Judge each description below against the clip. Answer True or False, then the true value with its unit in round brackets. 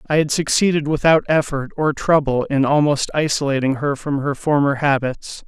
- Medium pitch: True (145 Hz)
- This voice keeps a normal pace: True (165 wpm)